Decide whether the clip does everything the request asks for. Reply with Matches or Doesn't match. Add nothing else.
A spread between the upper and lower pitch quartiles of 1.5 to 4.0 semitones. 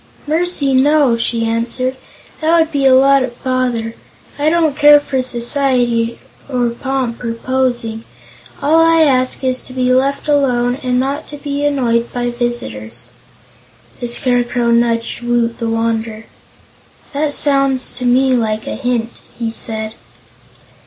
Matches